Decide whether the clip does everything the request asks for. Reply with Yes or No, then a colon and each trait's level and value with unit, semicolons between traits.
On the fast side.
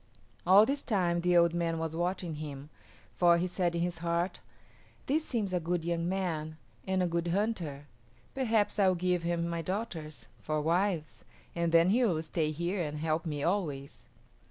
No: average, 180 wpm